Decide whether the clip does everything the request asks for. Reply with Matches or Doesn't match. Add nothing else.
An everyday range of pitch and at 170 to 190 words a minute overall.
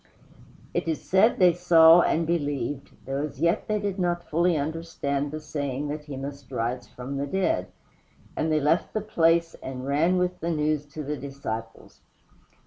Matches